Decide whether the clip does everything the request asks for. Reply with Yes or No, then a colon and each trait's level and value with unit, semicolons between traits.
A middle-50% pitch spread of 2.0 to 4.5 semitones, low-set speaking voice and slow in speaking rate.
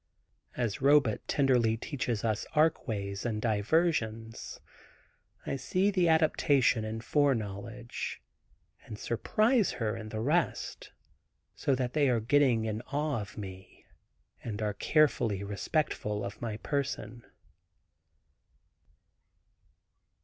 No: average, 5.1 semitones; low, 120 Hz; slow, 110 wpm